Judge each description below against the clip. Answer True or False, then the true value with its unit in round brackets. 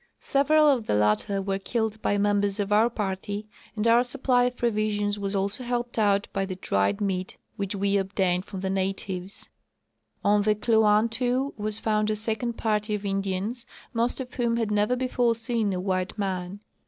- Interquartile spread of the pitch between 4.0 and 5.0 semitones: False (2.9 semitones)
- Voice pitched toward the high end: True (210 Hz)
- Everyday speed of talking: True (180 wpm)